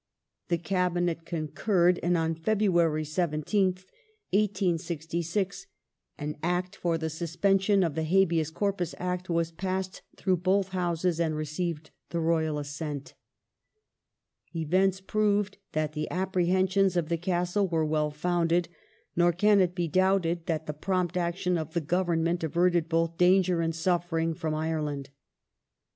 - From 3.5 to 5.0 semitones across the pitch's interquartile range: No, narrow, 2.4 semitones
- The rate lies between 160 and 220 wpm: No, slow, 135 wpm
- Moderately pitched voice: Yes, medium, 175 Hz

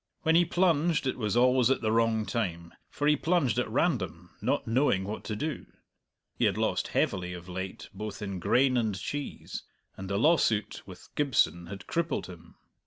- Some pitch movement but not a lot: No, wide, 7.0 semitones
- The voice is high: No, low, 110 Hz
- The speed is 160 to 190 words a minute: Yes, average, 180 wpm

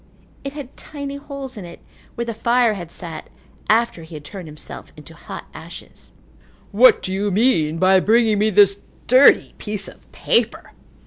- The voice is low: No, high, 210 Hz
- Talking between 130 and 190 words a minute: Yes, average, 170 wpm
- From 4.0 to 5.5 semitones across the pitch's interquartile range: Yes, average, 5.2 semitones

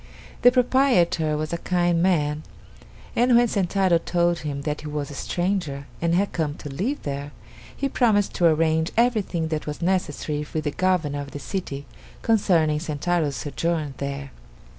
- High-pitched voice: No, medium, 165 Hz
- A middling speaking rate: Yes, average, 160 wpm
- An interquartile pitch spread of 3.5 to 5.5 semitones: Yes, average, 4.1 semitones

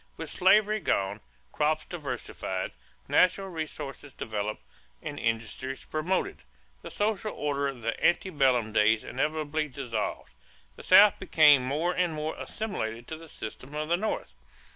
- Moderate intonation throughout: No, wide, 5.8 semitones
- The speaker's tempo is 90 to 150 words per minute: Yes, average, 140 wpm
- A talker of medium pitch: Yes, medium, 150 Hz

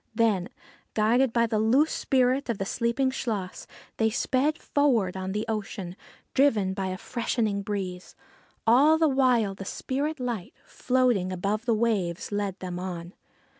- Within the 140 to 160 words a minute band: Yes, average, 150 wpm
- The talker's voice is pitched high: Yes, high, 220 Hz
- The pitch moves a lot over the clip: No, average, 4.8 semitones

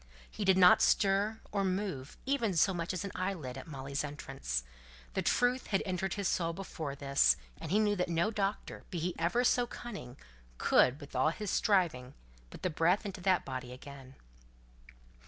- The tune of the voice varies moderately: No, wide, 6.1 semitones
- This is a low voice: No, medium, 180 Hz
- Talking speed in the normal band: Yes, average, 180 wpm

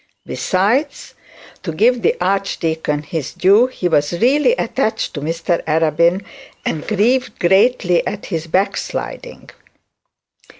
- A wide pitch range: Yes, wide, 6.0 semitones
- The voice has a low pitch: No, medium, 185 Hz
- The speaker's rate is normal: No, slow, 115 wpm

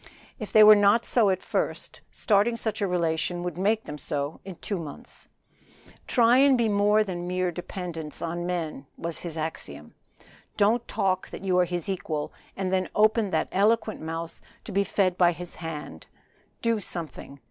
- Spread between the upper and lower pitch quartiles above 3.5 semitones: Yes, average, 4.0 semitones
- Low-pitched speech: No, medium, 185 Hz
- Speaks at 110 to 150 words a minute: No, average, 175 wpm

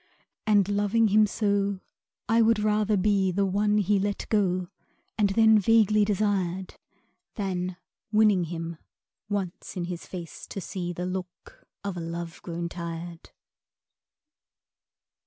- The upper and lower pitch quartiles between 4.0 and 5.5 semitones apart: No, average, 2.8 semitones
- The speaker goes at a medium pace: No, slow, 130 wpm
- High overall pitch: Yes, high, 195 Hz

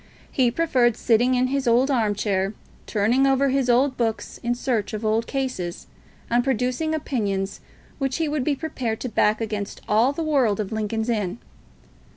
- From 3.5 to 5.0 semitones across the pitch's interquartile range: Yes, average, 3.8 semitones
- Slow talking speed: No, average, 175 wpm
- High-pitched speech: Yes, high, 240 Hz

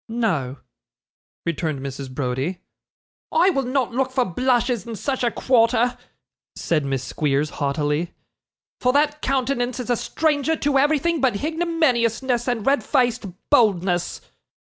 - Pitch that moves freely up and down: Yes, wide, 8.0 semitones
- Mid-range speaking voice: No, high, 240 Hz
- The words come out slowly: Yes, slow, 130 wpm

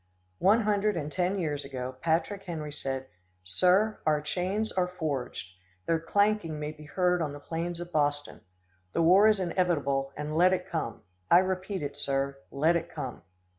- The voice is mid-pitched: Yes, medium, 165 Hz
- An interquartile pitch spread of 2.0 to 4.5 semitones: Yes, average, 4.2 semitones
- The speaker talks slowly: No, average, 170 wpm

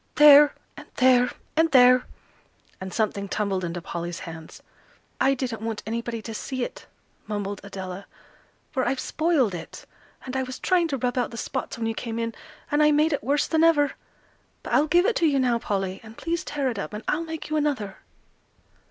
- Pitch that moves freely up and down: Yes, wide, 5.8 semitones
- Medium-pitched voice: No, very high, 250 Hz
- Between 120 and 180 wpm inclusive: No, average, 195 wpm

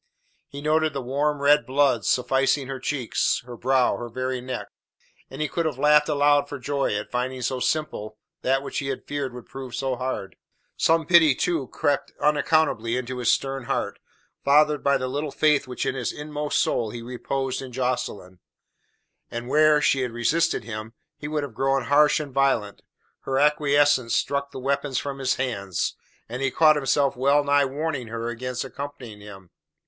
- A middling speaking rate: Yes, average, 180 wpm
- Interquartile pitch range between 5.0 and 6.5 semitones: No, average, 2.7 semitones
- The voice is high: No, low, 135 Hz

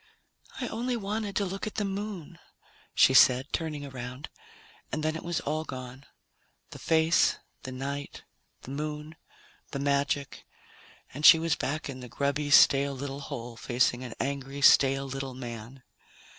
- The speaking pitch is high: No, medium, 140 Hz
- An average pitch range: Yes, average, 3.2 semitones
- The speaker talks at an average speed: Yes, average, 155 wpm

